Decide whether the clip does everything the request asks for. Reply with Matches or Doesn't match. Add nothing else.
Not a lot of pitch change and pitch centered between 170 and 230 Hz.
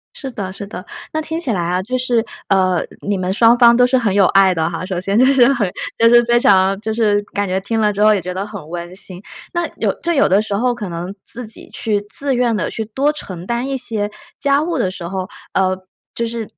Doesn't match